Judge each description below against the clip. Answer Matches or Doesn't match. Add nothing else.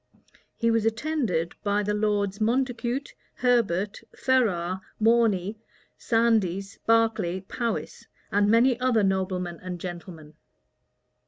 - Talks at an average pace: Doesn't match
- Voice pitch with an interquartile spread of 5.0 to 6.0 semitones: Doesn't match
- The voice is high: Matches